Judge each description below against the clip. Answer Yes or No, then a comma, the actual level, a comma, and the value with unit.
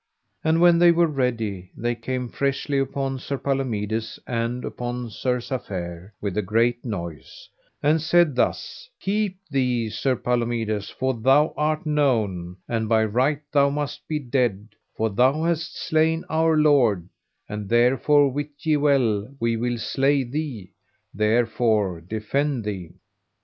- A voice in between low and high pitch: No, low, 125 Hz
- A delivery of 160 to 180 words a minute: No, average, 140 wpm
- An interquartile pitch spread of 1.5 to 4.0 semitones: No, average, 4.9 semitones